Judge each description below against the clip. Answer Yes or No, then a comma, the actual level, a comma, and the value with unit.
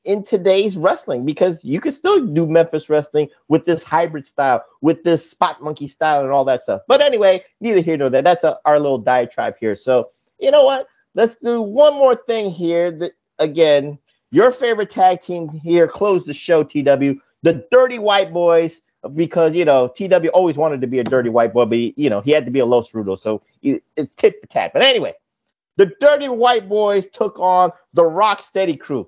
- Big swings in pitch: Yes, wide, 6.1 semitones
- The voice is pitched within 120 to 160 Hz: No, medium, 170 Hz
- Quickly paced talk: Yes, fast, 210 wpm